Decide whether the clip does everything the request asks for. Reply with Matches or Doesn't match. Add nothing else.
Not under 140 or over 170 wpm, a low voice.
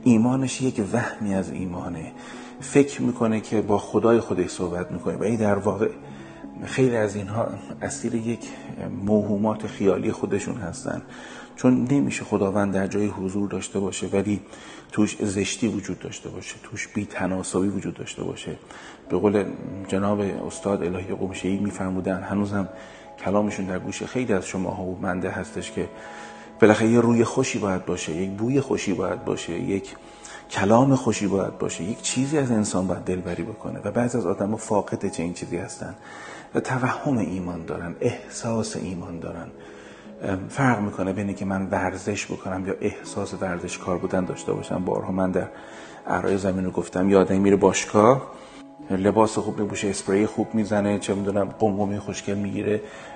Matches